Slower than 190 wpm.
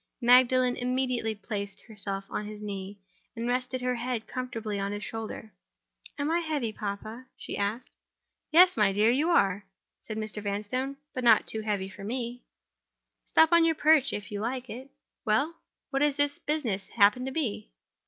Yes: average, 170 wpm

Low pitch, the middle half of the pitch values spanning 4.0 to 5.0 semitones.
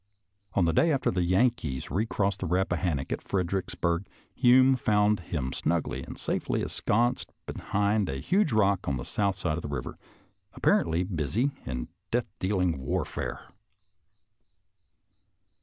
Yes: very low, 95 Hz; average, 4.4 semitones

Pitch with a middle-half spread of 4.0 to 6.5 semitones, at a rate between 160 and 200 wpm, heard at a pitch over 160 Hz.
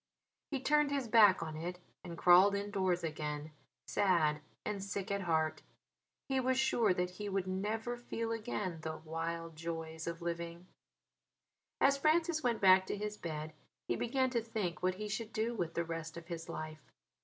Yes: average, 5.2 semitones; average, 175 wpm; medium, 185 Hz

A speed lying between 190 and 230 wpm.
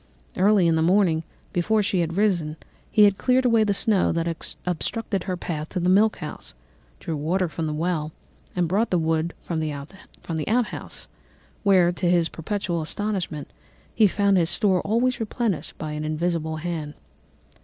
No: average, 165 wpm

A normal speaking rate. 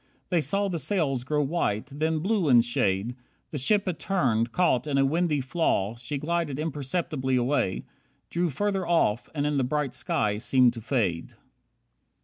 Yes: average, 165 wpm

